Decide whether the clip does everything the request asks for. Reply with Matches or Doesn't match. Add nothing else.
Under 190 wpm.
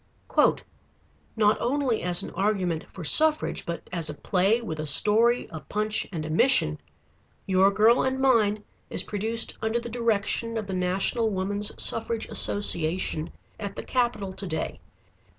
Matches